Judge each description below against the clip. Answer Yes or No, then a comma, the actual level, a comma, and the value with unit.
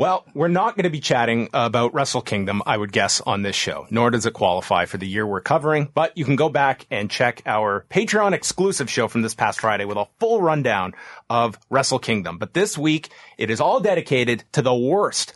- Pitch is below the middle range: Yes, low, 130 Hz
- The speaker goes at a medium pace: No, fast, 225 wpm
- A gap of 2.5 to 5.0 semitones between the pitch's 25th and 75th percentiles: No, wide, 5.6 semitones